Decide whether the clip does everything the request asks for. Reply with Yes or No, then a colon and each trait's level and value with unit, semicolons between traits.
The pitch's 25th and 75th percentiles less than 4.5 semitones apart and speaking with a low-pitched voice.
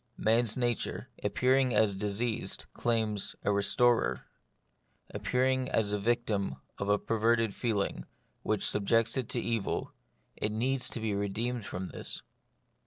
Yes: average, 2.9 semitones; low, 115 Hz